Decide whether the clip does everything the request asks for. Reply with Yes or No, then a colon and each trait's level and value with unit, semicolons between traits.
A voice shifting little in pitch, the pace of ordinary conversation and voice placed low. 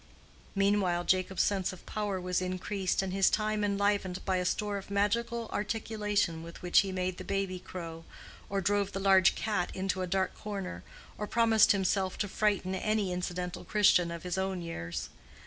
No: narrow, 2.1 semitones; average, 175 wpm; high, 190 Hz